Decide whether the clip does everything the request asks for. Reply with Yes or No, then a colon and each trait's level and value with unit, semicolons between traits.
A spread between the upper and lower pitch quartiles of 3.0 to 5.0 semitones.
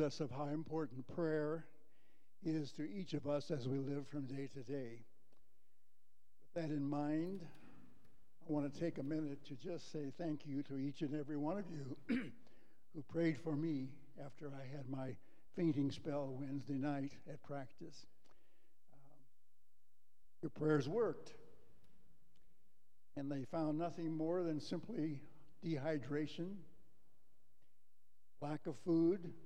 No: narrow, 2.4 semitones